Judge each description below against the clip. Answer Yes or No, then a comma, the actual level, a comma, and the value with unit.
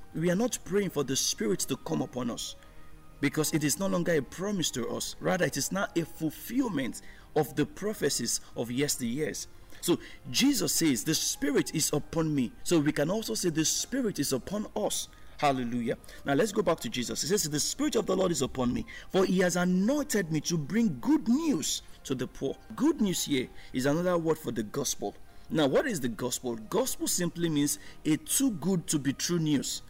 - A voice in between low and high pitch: Yes, medium, 160 Hz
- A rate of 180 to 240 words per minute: Yes, fast, 205 wpm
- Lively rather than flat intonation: Yes, wide, 6.7 semitones